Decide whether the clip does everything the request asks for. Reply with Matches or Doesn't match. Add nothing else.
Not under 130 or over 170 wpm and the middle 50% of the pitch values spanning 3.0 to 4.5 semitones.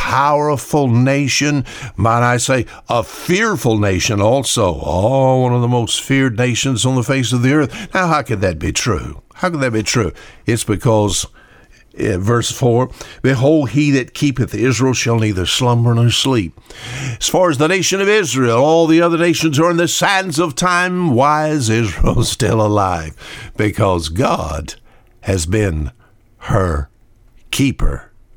Doesn't match